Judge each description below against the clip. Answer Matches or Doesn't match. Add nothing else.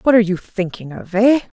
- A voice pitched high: Matches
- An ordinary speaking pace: Doesn't match